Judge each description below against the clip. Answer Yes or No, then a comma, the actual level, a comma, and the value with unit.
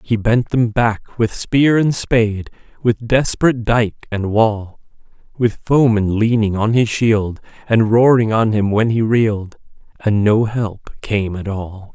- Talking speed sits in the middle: Yes, average, 160 wpm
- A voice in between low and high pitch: No, low, 110 Hz